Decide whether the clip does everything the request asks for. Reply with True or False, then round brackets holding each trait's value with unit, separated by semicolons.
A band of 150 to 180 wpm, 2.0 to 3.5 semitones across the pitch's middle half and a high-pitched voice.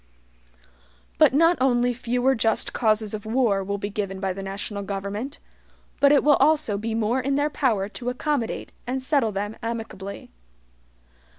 False (160 wpm; 4.6 semitones; 225 Hz)